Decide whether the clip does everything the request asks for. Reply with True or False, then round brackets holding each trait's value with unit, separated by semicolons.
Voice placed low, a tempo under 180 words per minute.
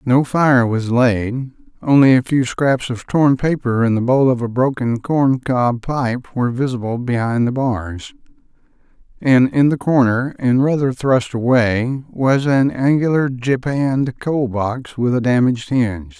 True (125 Hz; 160 wpm)